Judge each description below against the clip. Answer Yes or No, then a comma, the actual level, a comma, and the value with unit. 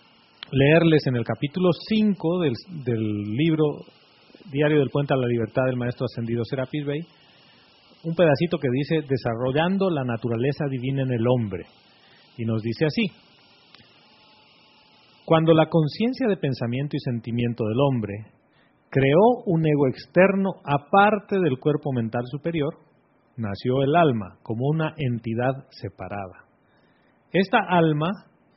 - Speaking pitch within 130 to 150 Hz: Yes, medium, 140 Hz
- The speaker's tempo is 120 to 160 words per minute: Yes, average, 130 wpm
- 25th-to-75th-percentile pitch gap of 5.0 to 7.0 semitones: Yes, average, 5.3 semitones